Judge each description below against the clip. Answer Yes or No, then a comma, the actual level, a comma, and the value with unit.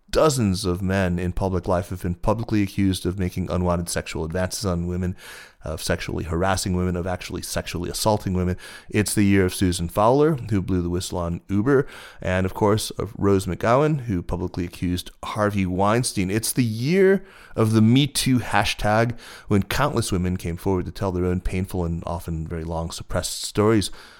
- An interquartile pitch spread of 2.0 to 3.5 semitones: Yes, average, 3.2 semitones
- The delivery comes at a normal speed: Yes, average, 180 wpm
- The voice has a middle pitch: No, very low, 95 Hz